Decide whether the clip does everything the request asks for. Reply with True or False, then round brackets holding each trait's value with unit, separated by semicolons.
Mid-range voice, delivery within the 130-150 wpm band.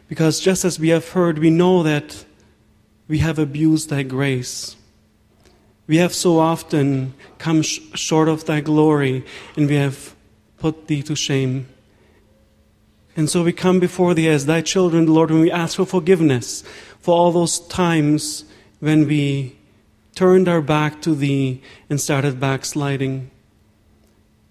True (150 Hz; 145 wpm)